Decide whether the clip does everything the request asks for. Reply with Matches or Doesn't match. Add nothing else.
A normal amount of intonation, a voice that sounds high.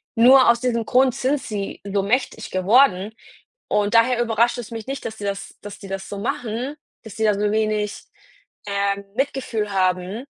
Matches